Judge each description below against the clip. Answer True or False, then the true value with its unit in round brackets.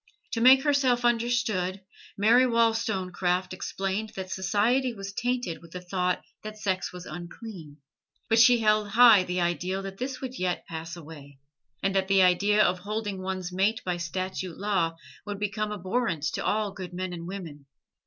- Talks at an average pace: True (165 wpm)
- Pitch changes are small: False (3.7 semitones)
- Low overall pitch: False (195 Hz)